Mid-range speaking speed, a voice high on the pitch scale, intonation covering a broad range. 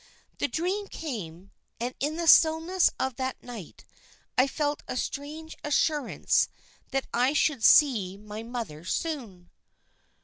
No: slow, 130 wpm; very high, 265 Hz; wide, 5.9 semitones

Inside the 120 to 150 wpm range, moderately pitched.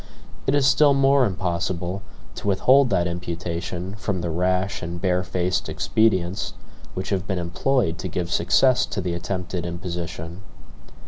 No: average, 140 wpm; very low, 90 Hz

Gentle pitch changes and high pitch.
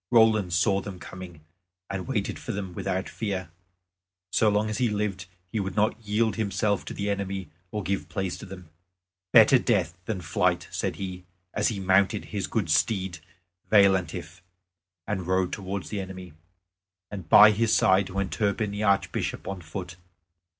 No: narrow, 2.3 semitones; low, 100 Hz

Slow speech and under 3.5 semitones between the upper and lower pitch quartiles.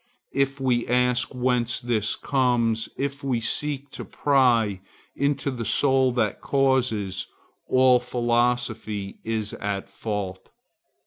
Yes: slow, 115 wpm; average, 3.0 semitones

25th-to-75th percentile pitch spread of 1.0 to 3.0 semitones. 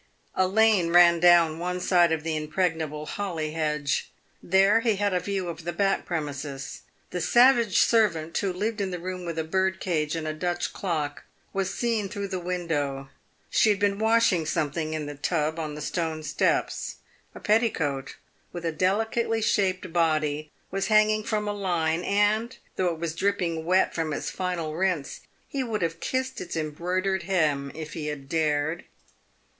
No: average, 4.0 semitones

